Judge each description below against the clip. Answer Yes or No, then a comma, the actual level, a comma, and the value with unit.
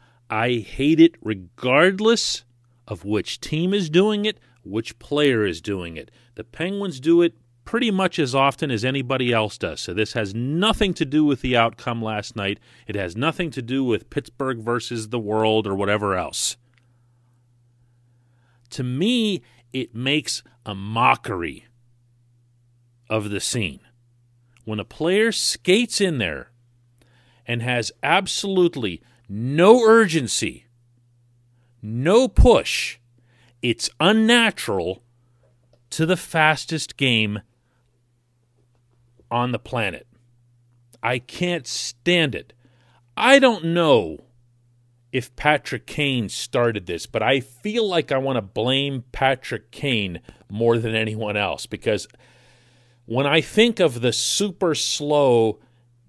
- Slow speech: Yes, slow, 125 wpm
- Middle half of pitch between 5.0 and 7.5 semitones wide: No, average, 3.8 semitones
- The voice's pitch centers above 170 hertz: No, low, 120 Hz